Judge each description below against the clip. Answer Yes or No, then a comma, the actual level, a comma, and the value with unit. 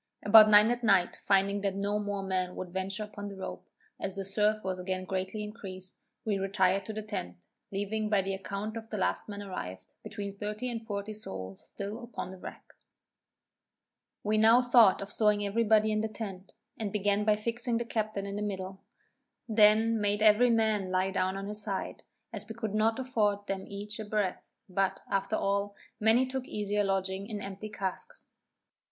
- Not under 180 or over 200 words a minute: Yes, average, 190 wpm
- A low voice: No, high, 205 Hz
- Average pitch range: No, narrow, 1.9 semitones